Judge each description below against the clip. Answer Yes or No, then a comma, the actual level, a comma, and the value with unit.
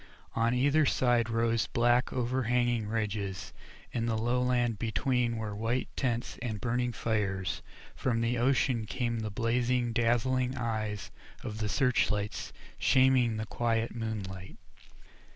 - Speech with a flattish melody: Yes, narrow, 2.1 semitones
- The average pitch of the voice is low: Yes, low, 115 Hz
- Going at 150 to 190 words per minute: No, slow, 135 wpm